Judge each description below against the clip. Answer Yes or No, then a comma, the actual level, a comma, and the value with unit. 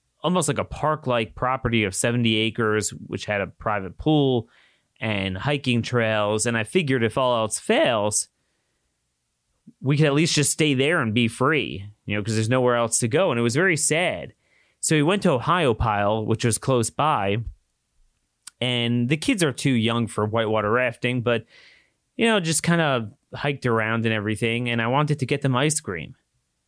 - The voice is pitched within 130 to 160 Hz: No, low, 120 Hz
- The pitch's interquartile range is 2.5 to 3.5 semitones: No, average, 4.3 semitones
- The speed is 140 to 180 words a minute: No, average, 190 wpm